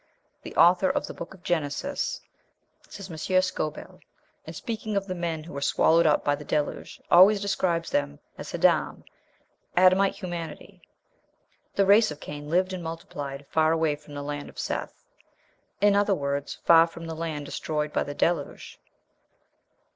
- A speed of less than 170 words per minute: Yes, average, 160 wpm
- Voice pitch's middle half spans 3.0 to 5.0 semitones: Yes, average, 4.0 semitones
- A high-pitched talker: No, medium, 165 Hz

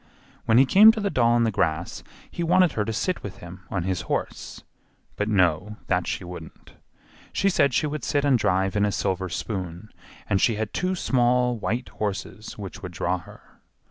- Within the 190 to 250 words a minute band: Yes, average, 200 wpm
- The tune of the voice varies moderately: No, wide, 5.7 semitones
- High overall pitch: No, low, 105 Hz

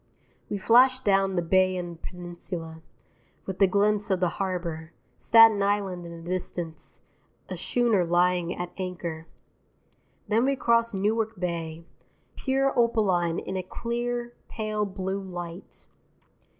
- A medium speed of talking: No, slow, 125 wpm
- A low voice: No, high, 190 Hz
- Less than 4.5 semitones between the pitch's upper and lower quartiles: Yes, average, 3.8 semitones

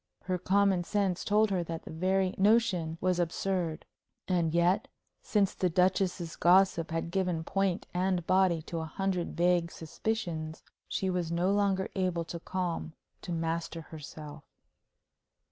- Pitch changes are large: No, narrow, 2.4 semitones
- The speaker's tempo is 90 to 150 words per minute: Yes, average, 145 wpm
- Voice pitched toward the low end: No, medium, 180 Hz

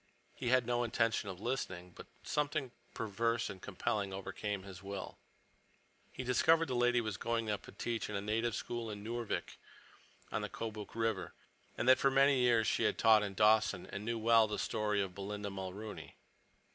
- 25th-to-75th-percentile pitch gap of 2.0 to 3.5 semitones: Yes, average, 2.9 semitones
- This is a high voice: No, low, 110 Hz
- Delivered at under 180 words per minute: No, average, 185 wpm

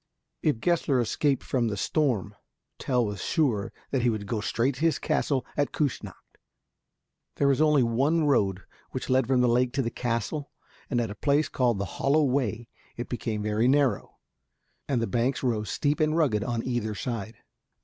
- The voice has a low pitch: Yes, low, 125 Hz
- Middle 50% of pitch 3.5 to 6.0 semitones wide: Yes, average, 3.9 semitones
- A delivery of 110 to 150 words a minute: No, average, 180 wpm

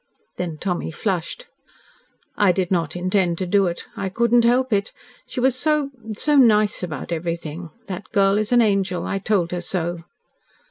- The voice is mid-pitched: No, high, 195 Hz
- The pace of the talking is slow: No, average, 175 wpm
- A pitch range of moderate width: Yes, average, 4.0 semitones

